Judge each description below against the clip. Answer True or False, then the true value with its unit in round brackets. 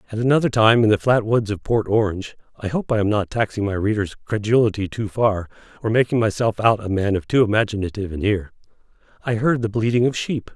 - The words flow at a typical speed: False (215 wpm)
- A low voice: True (110 Hz)